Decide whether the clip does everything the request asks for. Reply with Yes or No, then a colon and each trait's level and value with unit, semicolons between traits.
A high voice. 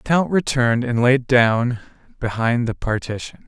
No: low, 125 Hz